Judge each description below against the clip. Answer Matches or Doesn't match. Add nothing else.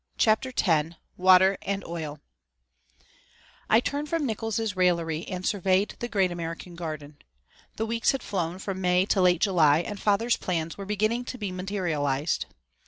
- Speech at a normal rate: Matches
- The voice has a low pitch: Doesn't match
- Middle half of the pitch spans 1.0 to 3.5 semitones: Doesn't match